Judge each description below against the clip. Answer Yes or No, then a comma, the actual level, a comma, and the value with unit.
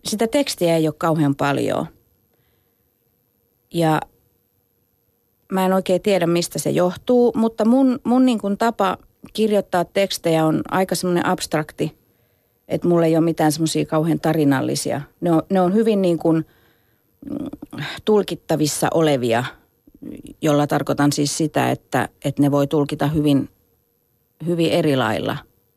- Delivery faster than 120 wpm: Yes, average, 130 wpm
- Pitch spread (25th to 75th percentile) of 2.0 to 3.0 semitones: No, average, 4.9 semitones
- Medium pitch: Yes, medium, 160 Hz